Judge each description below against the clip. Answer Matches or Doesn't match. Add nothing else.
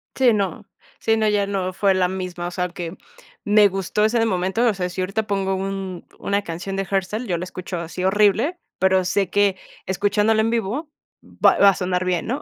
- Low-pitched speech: Doesn't match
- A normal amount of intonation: Doesn't match